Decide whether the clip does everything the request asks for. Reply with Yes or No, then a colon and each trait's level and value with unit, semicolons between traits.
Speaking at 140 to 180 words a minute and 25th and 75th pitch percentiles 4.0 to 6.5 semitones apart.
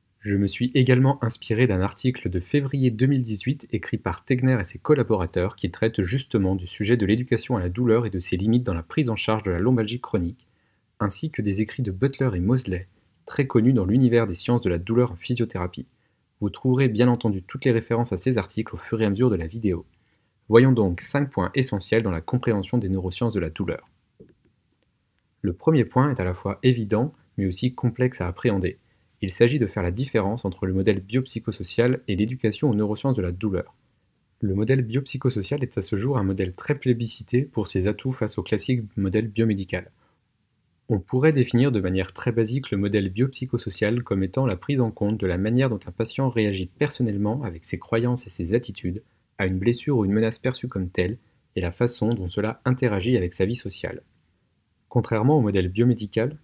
No: average, 205 wpm; average, 4.3 semitones